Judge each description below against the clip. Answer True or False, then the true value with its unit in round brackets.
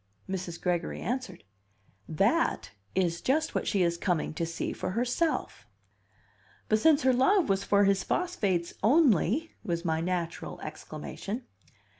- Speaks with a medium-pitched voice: False (195 Hz)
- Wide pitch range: True (7.0 semitones)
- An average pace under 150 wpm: True (140 wpm)